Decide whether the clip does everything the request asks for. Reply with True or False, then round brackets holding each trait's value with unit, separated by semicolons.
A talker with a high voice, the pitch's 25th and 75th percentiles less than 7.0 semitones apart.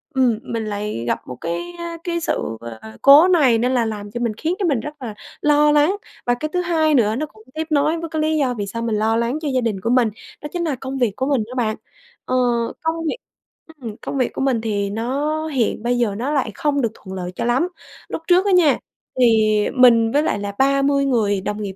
True (250 Hz; 5.5 semitones)